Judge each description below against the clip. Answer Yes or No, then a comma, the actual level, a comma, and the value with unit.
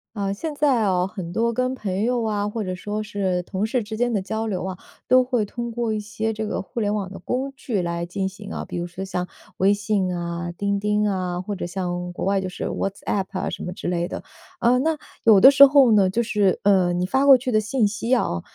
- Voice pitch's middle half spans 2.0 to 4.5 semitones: Yes, average, 3.9 semitones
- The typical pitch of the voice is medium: No, high, 205 Hz